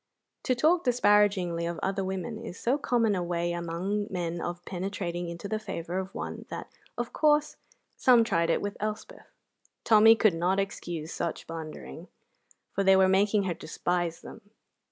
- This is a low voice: No, high, 190 Hz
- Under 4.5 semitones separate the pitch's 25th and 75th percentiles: Yes, average, 3.9 semitones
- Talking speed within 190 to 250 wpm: No, average, 165 wpm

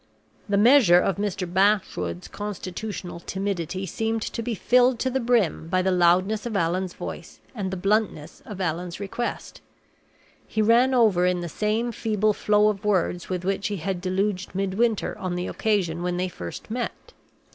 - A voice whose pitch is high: Yes, high, 195 Hz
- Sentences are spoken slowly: No, average, 170 wpm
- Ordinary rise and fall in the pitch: Yes, average, 3.3 semitones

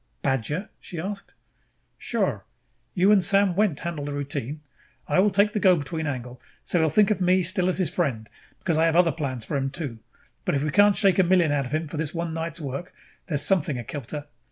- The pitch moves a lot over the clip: No, average, 4.4 semitones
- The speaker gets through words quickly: Yes, fast, 225 wpm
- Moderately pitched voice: Yes, medium, 165 Hz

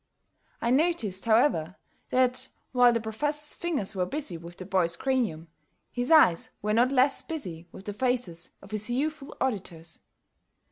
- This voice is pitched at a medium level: No, high, 230 Hz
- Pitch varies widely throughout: Yes, wide, 6.2 semitones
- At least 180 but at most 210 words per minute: No, average, 150 wpm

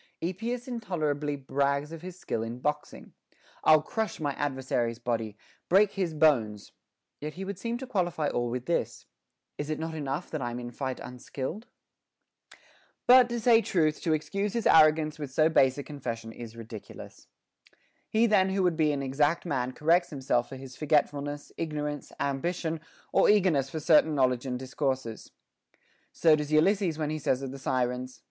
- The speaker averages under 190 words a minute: Yes, average, 175 wpm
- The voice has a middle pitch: Yes, medium, 150 Hz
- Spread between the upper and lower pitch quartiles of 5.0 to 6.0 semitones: No, average, 4.6 semitones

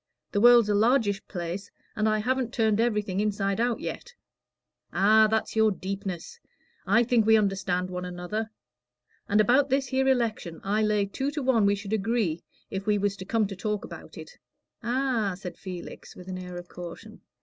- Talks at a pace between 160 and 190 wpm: Yes, average, 180 wpm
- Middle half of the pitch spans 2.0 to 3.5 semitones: Yes, average, 3.1 semitones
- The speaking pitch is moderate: No, high, 210 Hz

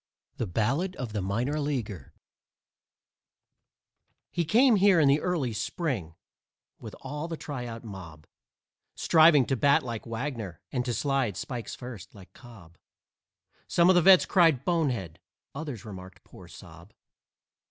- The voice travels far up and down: Yes, wide, 6.8 semitones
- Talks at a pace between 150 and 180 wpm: No, slow, 135 wpm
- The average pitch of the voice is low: Yes, low, 130 Hz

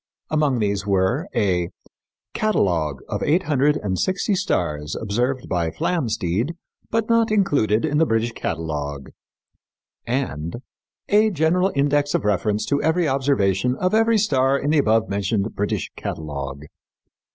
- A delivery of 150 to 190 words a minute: No, slow, 135 wpm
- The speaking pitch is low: Yes, low, 125 Hz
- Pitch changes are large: Yes, wide, 8.7 semitones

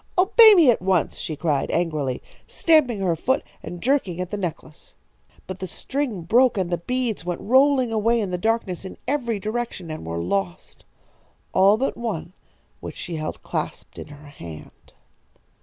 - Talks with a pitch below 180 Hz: No, high, 195 Hz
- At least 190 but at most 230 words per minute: No, average, 170 wpm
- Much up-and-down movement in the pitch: Yes, wide, 6.2 semitones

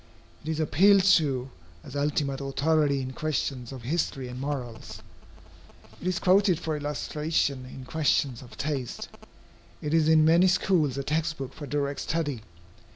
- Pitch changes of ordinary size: Yes, average, 3.1 semitones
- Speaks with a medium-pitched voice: Yes, medium, 145 Hz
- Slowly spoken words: No, average, 155 wpm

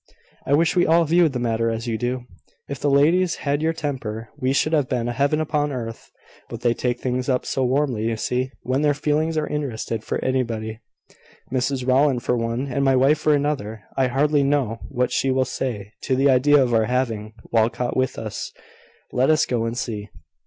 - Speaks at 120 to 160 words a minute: No, average, 200 wpm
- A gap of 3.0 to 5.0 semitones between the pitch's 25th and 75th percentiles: Yes, average, 3.6 semitones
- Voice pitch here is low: Yes, low, 130 Hz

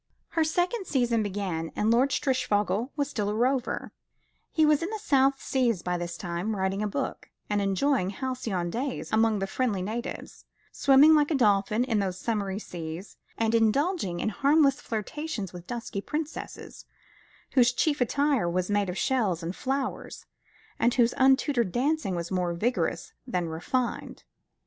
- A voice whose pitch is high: Yes, high, 230 Hz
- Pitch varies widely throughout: Yes, wide, 5.8 semitones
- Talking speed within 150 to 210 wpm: Yes, average, 160 wpm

